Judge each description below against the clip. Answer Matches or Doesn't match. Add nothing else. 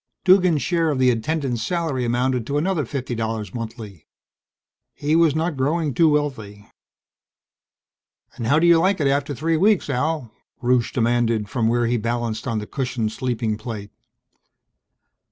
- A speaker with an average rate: Matches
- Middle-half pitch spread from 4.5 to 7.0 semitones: Matches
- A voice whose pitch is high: Doesn't match